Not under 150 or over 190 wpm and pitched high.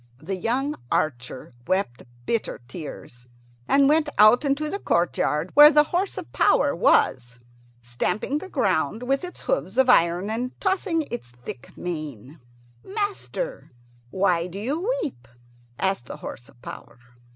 No: average, 140 wpm; high, 210 Hz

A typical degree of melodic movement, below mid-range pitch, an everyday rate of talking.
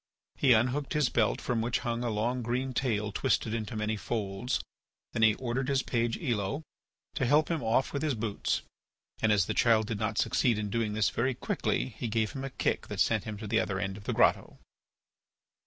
No: average, 3.0 semitones; low, 115 Hz; fast, 210 wpm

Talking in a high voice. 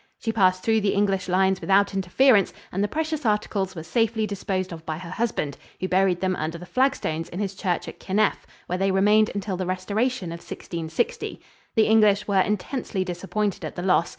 Yes: high, 195 Hz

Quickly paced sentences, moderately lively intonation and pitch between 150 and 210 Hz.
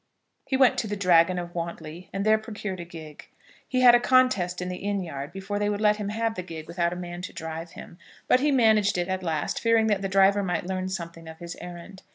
Yes: fast, 245 wpm; average, 3.5 semitones; high, 190 Hz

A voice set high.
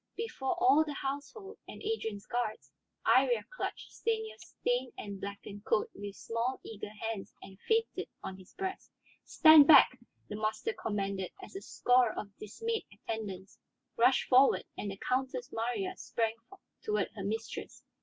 Yes: high, 245 Hz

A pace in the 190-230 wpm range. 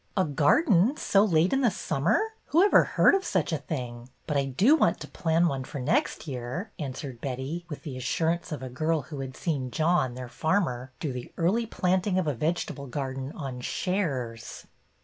Yes: average, 200 wpm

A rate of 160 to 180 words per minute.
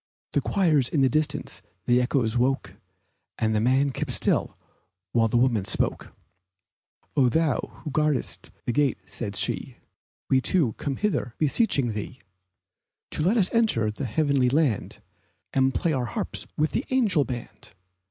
No: average, 150 wpm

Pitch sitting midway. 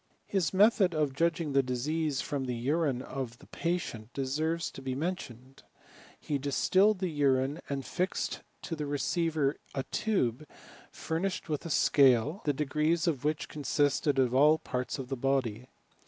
Yes: medium, 145 Hz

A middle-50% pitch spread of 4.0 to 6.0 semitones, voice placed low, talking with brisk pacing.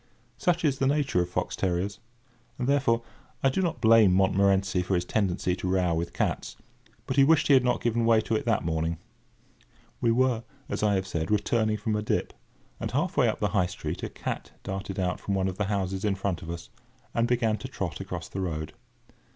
Yes: average, 4.4 semitones; low, 100 Hz; fast, 215 wpm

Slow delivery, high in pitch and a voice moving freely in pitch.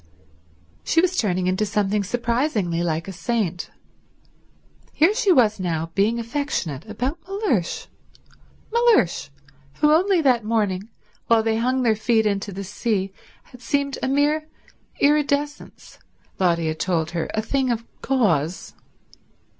Yes: slow, 130 wpm; high, 225 Hz; wide, 7.1 semitones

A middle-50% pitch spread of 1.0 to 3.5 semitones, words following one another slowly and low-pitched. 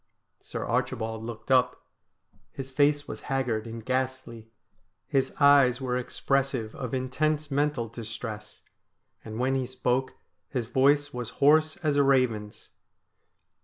Yes: average, 3.1 semitones; slow, 130 wpm; low, 130 Hz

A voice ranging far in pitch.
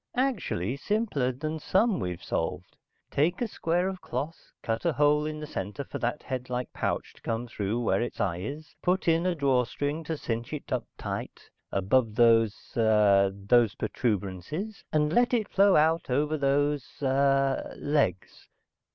Yes: wide, 5.7 semitones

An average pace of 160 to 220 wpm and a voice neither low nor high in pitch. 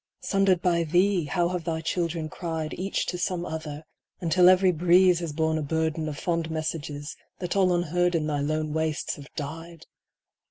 Yes: average, 175 wpm; medium, 165 Hz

